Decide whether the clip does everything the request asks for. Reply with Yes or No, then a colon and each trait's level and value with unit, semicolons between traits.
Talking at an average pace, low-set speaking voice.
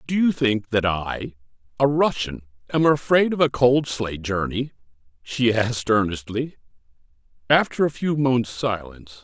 Yes: average, 145 wpm; low, 120 Hz